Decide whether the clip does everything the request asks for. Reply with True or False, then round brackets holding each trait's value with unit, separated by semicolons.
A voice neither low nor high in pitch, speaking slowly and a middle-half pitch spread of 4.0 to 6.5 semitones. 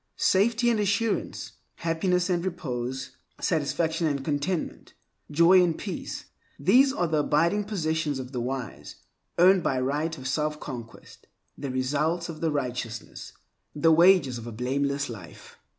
True (155 Hz; 130 wpm; 5.1 semitones)